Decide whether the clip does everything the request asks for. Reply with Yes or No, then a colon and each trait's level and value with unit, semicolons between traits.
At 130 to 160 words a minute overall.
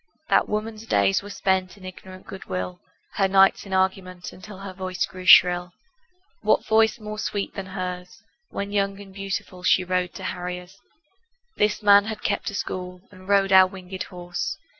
No: average, 175 wpm